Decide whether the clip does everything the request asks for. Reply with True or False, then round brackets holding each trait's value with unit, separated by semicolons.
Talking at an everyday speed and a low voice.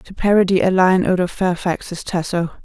False (180 wpm; 180 Hz)